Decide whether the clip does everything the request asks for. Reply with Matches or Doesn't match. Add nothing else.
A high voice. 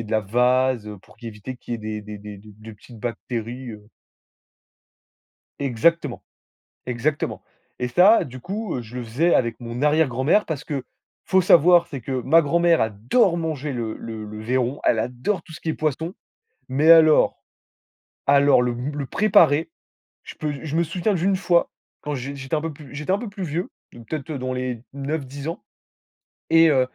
Doesn't match